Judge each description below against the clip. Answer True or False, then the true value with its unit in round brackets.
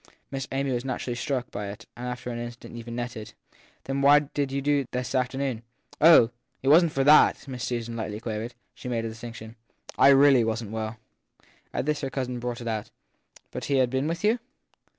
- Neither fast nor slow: False (220 wpm)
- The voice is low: True (125 Hz)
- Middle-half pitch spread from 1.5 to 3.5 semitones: True (2.9 semitones)